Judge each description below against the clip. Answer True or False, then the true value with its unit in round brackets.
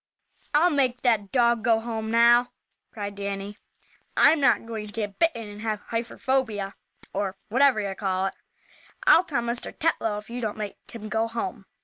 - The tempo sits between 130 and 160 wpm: False (170 wpm)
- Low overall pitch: False (225 Hz)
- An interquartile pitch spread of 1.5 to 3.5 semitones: True (2.7 semitones)